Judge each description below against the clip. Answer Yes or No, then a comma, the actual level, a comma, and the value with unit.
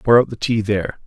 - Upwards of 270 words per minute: Yes, fast, 280 wpm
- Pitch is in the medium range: No, low, 110 Hz